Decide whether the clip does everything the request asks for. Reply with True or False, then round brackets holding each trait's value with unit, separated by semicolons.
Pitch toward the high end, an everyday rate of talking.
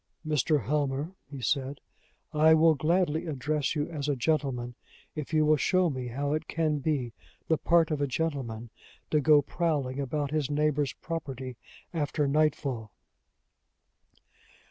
False (150 Hz; 145 wpm)